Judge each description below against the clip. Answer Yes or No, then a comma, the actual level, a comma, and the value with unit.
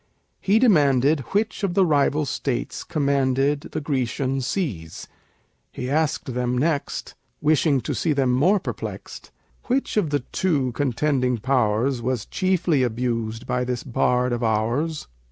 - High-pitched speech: No, low, 135 Hz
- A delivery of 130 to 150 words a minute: Yes, slow, 135 wpm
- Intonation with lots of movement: No, average, 3.9 semitones